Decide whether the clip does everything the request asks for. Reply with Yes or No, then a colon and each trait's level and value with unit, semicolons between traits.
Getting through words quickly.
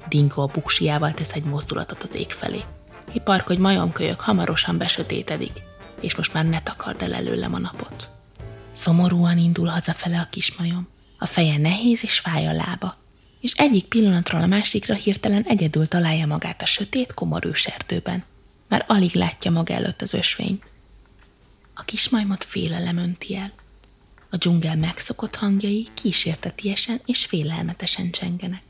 No: average, 145 wpm